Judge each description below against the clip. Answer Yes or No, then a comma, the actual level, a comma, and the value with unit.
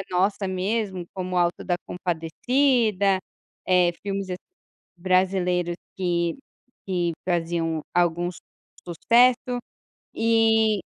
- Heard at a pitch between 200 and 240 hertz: No, medium, 185 Hz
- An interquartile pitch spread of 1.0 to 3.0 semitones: No, average, 3.5 semitones